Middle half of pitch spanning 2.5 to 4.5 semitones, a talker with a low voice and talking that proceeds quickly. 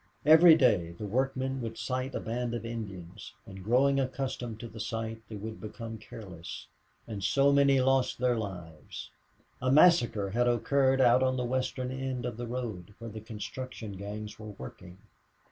No: average, 3.6 semitones; low, 120 Hz; average, 170 wpm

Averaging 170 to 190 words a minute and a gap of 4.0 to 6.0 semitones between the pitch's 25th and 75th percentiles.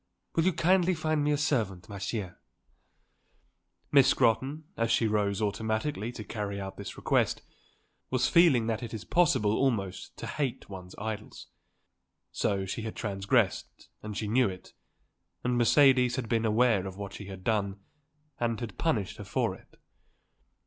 No: average, 155 wpm; average, 4.5 semitones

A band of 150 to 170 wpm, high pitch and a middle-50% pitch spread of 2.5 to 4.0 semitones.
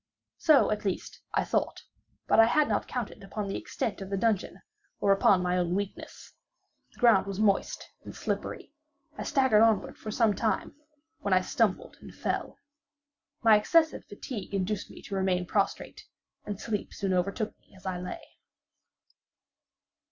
Yes: average, 160 wpm; high, 205 Hz; average, 2.8 semitones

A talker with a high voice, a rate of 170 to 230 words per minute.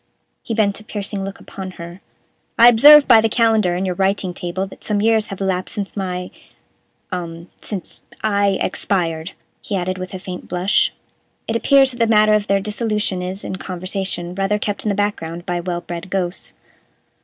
Yes: high, 195 Hz; average, 185 wpm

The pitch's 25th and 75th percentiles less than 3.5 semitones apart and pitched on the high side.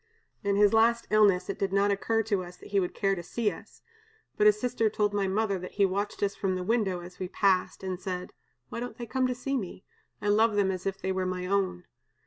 Yes: narrow, 2.5 semitones; high, 200 Hz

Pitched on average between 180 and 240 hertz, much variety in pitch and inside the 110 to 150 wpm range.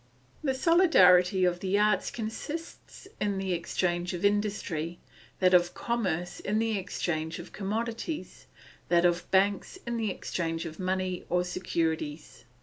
No: medium, 185 Hz; average, 3.4 semitones; average, 140 wpm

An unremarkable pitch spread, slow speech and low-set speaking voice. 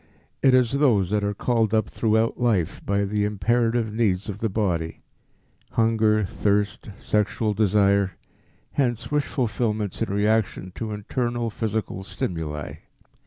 No: narrow, 2.3 semitones; slow, 130 wpm; low, 105 Hz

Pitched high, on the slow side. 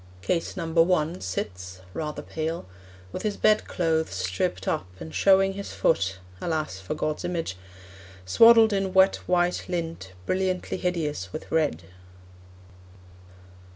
No: medium, 165 Hz; slow, 120 wpm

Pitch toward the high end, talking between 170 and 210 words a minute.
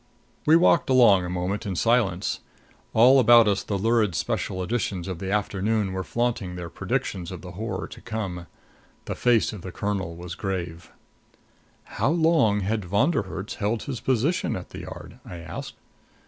No: low, 100 Hz; average, 175 wpm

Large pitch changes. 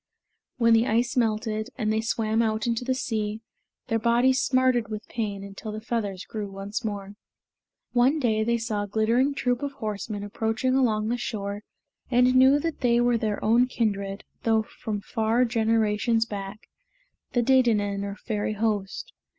No: narrow, 2.4 semitones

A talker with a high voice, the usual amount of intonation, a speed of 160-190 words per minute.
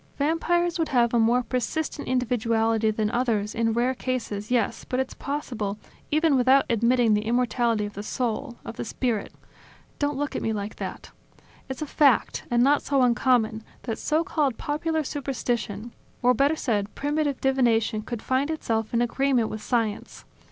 Yes: high, 245 Hz; average, 3.7 semitones; average, 165 wpm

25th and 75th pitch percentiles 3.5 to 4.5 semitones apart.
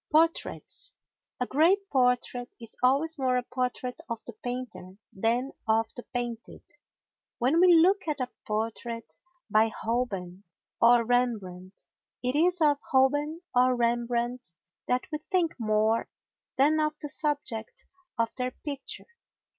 Yes: average, 4.1 semitones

